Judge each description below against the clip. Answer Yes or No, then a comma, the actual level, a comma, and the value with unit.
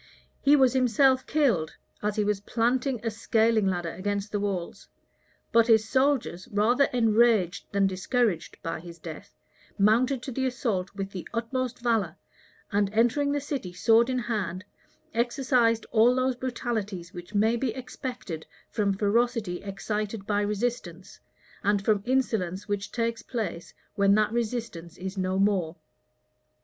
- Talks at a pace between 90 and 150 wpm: Yes, average, 145 wpm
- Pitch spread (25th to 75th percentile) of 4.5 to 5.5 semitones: No, average, 3.8 semitones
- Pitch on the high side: Yes, high, 220 Hz